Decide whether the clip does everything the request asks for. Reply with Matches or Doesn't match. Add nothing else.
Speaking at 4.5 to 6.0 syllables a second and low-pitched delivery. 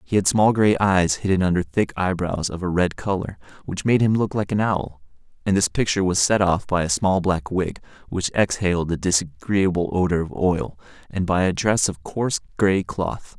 Matches